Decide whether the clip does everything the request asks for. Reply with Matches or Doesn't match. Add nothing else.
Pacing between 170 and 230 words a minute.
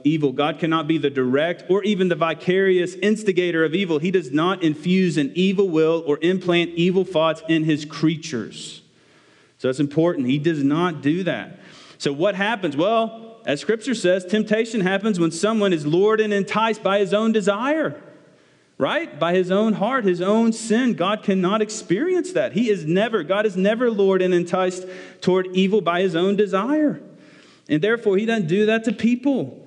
Matches